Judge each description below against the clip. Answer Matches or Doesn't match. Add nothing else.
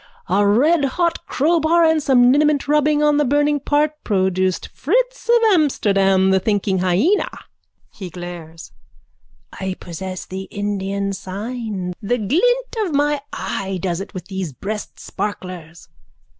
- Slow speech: Matches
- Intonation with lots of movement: Matches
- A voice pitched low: Doesn't match